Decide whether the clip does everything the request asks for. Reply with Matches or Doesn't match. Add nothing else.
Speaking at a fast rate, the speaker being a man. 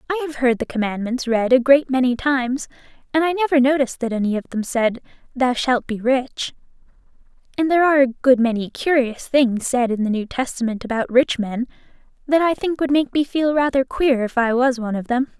Doesn't match